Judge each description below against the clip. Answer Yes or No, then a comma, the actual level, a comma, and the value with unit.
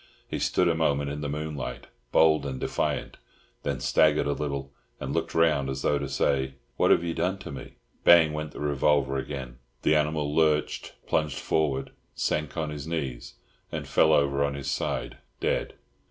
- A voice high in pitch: No, very low, 75 Hz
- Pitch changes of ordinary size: No, narrow, 2.0 semitones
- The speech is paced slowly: No, average, 180 wpm